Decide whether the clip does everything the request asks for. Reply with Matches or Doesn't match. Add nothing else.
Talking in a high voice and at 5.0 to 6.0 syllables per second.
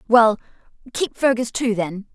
Doesn't match